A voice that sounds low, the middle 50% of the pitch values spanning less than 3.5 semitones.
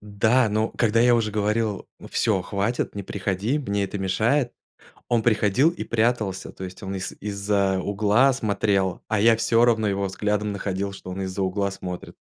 Yes: low, 105 Hz; narrow, 2.6 semitones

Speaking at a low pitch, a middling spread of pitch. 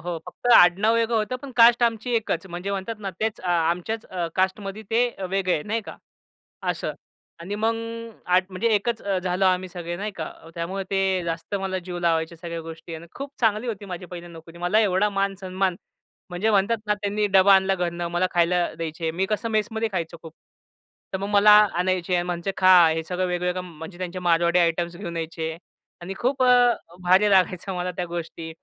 No: medium, 185 Hz; average, 3.1 semitones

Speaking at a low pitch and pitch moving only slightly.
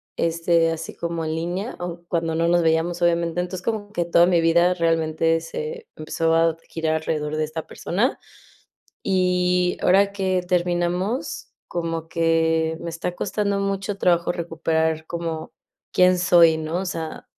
No: medium, 170 Hz; narrow, 1.8 semitones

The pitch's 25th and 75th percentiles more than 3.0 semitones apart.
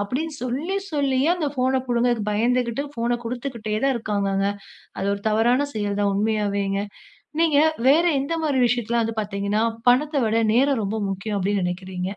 Yes: average, 4.5 semitones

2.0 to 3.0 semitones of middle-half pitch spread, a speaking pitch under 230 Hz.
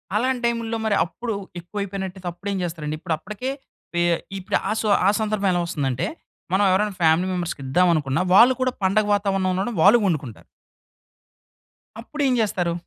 No: average, 3.7 semitones; high, 190 Hz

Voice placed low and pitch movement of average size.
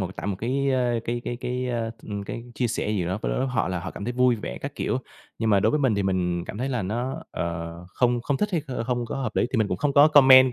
Yes: low, 120 Hz; average, 4.3 semitones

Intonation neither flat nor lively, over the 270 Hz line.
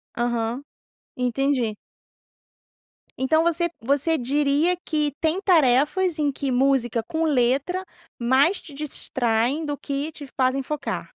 Yes: average, 3.8 semitones; very high, 280 Hz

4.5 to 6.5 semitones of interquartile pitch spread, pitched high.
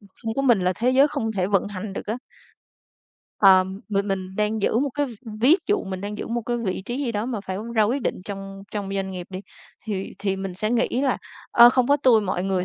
No: average, 3.8 semitones; high, 210 Hz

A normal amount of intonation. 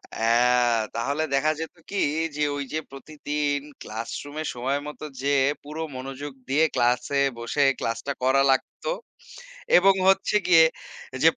Yes: average, 3.3 semitones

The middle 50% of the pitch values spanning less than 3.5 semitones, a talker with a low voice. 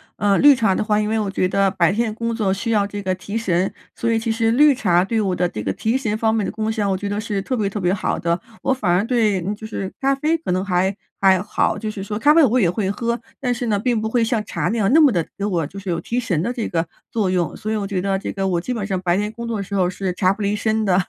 No: average, 3.1 semitones; high, 205 Hz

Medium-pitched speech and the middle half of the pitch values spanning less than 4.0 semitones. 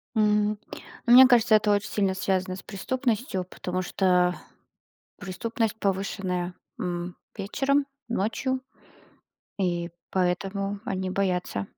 No: high, 195 Hz; average, 3.0 semitones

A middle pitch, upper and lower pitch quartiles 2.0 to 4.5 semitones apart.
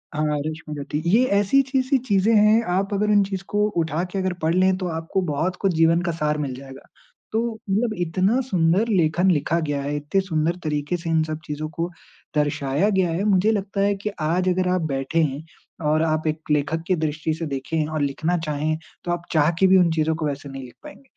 Yes: medium, 165 Hz; average, 3.8 semitones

